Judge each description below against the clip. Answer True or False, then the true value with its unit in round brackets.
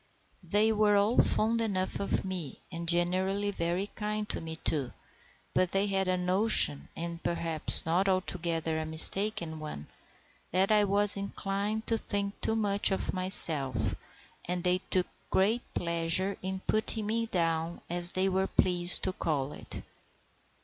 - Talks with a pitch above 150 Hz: True (185 Hz)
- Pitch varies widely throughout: False (3.3 semitones)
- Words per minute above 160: False (150 wpm)